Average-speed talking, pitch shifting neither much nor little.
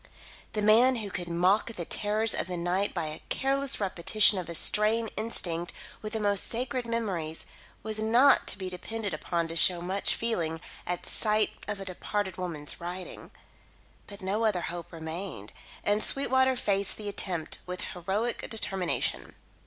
Yes: average, 160 wpm; average, 3.9 semitones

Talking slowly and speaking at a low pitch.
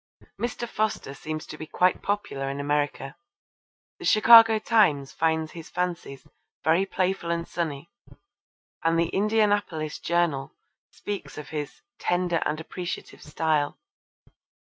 No: slow, 120 wpm; medium, 165 Hz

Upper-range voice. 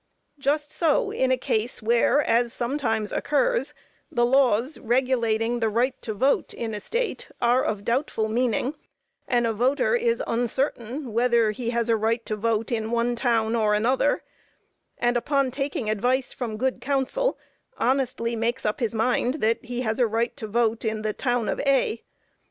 Yes: high, 240 Hz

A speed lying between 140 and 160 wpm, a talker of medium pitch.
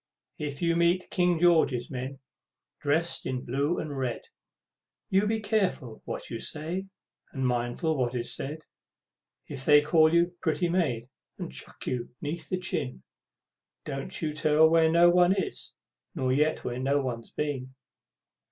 Yes: average, 150 wpm; medium, 150 Hz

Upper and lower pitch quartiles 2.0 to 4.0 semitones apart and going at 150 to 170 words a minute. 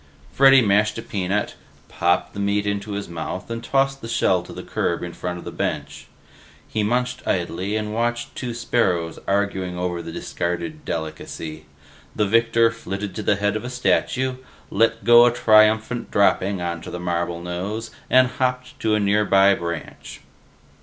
No: average, 4.6 semitones; average, 165 wpm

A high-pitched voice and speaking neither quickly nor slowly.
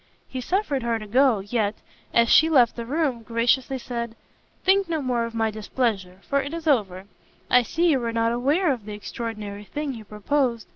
Yes: high, 235 Hz; average, 195 wpm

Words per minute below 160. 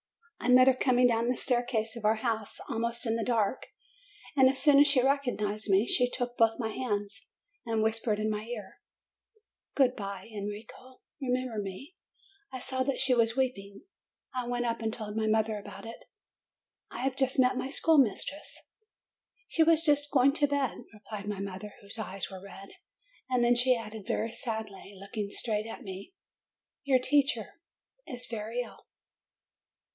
No: average, 170 wpm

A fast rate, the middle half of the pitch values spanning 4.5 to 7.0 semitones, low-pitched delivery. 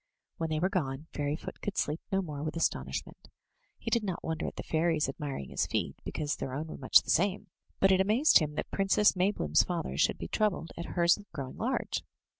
No: fast, 210 wpm; average, 4.8 semitones; medium, 165 Hz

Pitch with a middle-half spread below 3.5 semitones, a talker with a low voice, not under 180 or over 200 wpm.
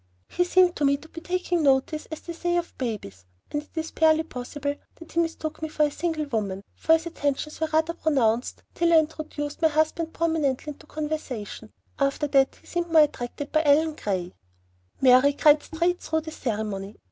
No: average, 3.0 semitones; very high, 305 Hz; average, 195 wpm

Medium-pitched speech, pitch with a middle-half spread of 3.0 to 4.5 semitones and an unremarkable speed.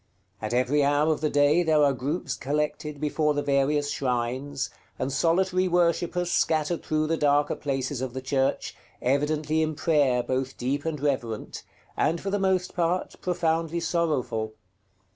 Yes: medium, 150 Hz; average, 3.3 semitones; average, 155 wpm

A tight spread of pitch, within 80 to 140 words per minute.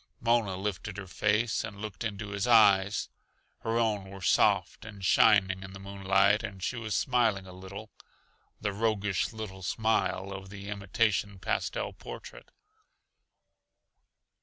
Yes: narrow, 2.2 semitones; slow, 135 wpm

